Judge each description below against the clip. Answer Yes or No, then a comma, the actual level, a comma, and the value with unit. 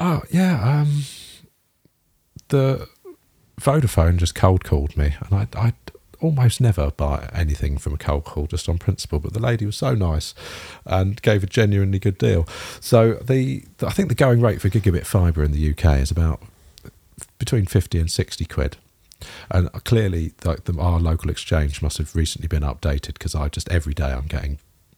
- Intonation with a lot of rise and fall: Yes, wide, 6.6 semitones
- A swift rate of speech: No, average, 180 wpm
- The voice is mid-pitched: No, very low, 95 Hz